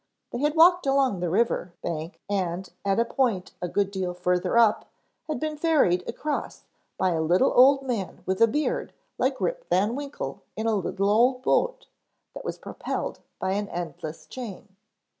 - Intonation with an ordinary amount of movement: No, wide, 7.0 semitones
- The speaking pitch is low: No, high, 210 Hz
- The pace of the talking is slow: No, average, 175 wpm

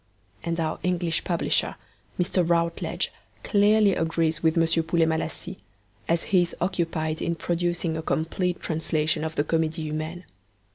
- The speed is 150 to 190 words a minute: No, average, 140 wpm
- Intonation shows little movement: Yes, narrow, 1.6 semitones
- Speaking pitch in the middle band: Yes, medium, 165 Hz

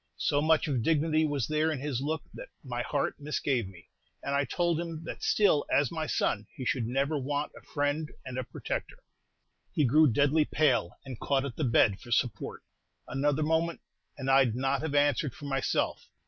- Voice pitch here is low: No, medium, 145 Hz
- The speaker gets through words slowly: No, average, 195 wpm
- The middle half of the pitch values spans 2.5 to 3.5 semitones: Yes, average, 2.9 semitones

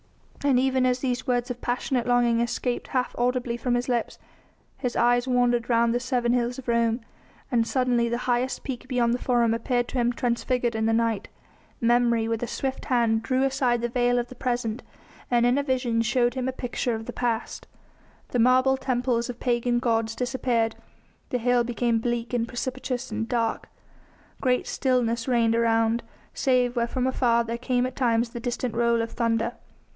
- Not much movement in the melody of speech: Yes, narrow, 1.3 semitones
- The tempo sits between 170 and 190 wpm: Yes, average, 185 wpm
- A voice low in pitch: No, high, 240 Hz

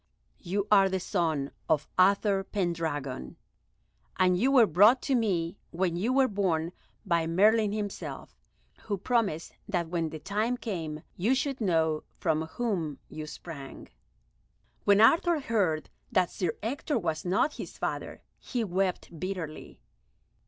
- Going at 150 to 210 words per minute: No, average, 140 wpm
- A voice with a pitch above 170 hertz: Yes, medium, 185 Hz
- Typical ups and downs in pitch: Yes, average, 4.9 semitones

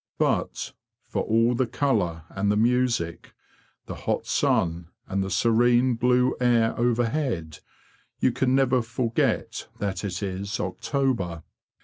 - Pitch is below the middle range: Yes, low, 115 Hz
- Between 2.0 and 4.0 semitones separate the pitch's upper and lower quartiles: No, average, 4.5 semitones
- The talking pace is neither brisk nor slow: No, slow, 125 wpm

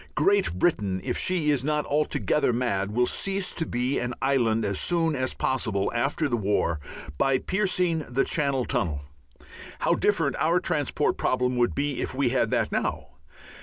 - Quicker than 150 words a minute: Yes, average, 165 wpm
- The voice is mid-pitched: No, low, 130 Hz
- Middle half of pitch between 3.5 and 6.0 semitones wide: Yes, average, 4.5 semitones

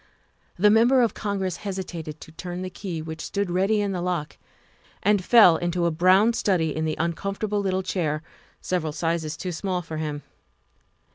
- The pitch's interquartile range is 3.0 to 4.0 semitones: Yes, average, 3.5 semitones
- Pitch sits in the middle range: Yes, medium, 180 Hz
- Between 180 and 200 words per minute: No, average, 170 wpm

